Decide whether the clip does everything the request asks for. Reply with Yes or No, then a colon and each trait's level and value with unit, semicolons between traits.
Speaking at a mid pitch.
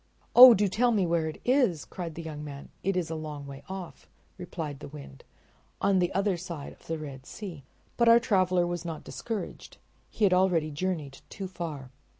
Yes: medium, 175 Hz